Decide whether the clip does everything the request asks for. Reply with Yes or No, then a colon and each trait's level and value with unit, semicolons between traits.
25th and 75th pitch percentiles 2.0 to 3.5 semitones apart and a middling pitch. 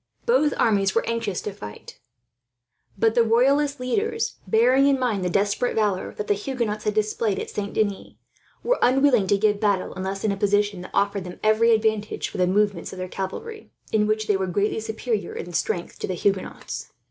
No: average, 2.9 semitones; high, 210 Hz